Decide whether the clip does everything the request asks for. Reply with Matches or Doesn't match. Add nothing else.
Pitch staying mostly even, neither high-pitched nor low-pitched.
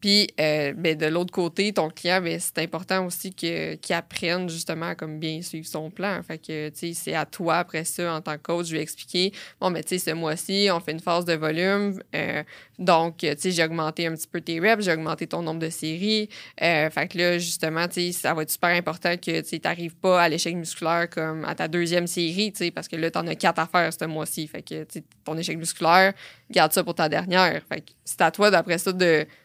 Matches